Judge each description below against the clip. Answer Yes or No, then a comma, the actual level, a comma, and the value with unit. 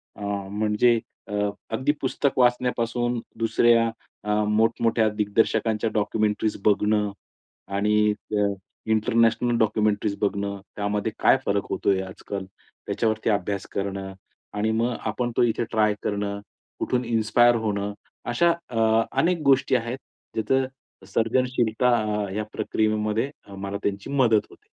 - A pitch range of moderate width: No, narrow, 2.3 semitones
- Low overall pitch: Yes, low, 110 Hz